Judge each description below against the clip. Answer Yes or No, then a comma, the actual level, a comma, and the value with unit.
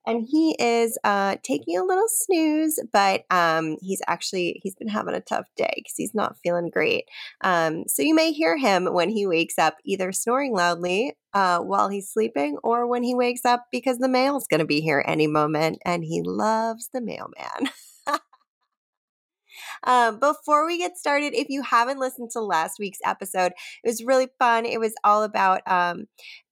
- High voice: Yes, high, 225 Hz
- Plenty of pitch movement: Yes, wide, 6.9 semitones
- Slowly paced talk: No, average, 185 wpm